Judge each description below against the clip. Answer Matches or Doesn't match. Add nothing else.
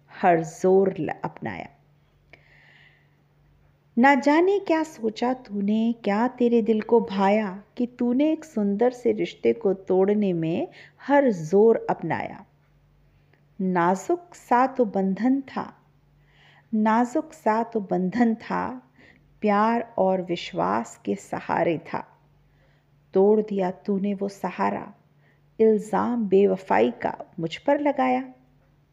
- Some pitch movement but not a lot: Doesn't match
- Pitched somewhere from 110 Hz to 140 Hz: Doesn't match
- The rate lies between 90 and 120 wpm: Matches